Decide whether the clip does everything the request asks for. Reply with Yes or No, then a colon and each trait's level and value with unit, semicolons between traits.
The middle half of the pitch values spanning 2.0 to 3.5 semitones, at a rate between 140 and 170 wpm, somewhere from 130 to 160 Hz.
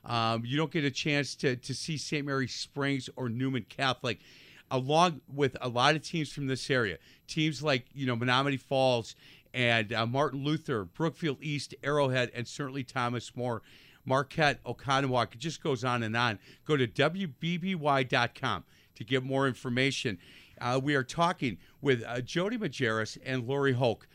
Yes: average, 3.0 semitones; average, 165 wpm; low, 135 Hz